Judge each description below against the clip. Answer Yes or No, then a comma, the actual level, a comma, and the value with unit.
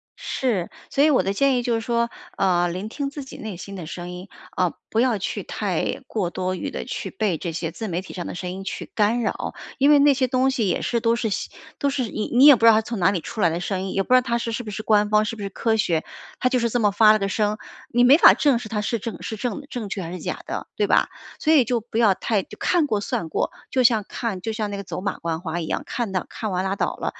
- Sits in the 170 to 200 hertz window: No, high, 215 Hz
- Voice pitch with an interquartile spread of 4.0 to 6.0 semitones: Yes, average, 4.3 semitones